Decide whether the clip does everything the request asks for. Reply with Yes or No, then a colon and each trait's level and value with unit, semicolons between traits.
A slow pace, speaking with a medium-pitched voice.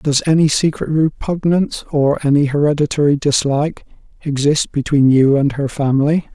Yes: slow, 130 wpm; medium, 145 Hz